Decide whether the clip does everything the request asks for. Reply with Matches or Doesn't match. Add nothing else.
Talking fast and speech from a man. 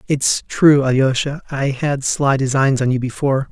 Doesn't match